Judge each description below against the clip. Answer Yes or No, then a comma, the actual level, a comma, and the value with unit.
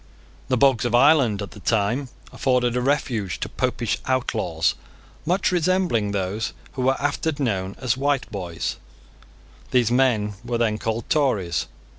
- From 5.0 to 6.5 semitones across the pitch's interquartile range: No, average, 4.2 semitones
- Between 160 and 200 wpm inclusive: No, average, 145 wpm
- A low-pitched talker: Yes, low, 120 Hz